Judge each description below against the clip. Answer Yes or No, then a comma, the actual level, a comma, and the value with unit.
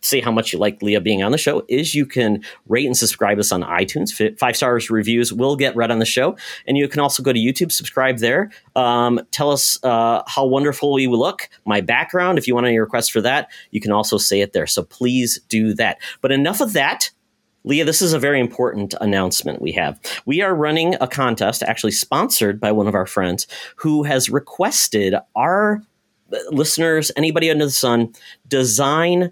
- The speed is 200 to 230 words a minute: Yes, fast, 205 wpm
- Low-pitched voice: Yes, low, 130 Hz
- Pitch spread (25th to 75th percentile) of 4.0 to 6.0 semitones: Yes, average, 4.7 semitones